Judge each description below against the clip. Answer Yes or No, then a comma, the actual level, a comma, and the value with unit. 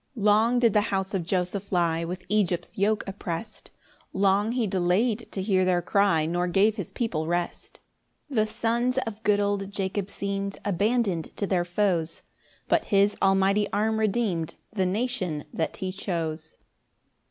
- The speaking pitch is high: Yes, high, 195 Hz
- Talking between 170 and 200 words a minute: No, average, 160 wpm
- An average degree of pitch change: Yes, average, 3.0 semitones